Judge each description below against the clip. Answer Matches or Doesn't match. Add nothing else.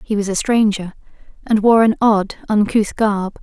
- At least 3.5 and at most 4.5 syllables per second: Matches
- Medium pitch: Doesn't match